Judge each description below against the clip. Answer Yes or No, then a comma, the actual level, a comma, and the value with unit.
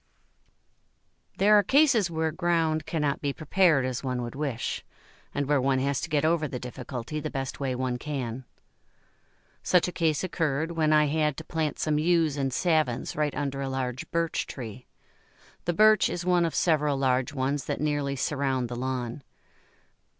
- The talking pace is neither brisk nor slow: Yes, average, 170 wpm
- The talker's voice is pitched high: No, medium, 145 Hz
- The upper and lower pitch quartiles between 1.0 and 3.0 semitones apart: No, average, 3.6 semitones